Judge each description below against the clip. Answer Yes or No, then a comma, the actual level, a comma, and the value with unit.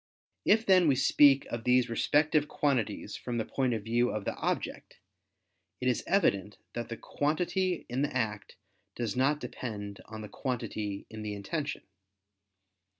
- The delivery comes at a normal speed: Yes, average, 155 wpm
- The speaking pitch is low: Yes, low, 125 Hz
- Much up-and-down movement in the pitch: No, average, 4.9 semitones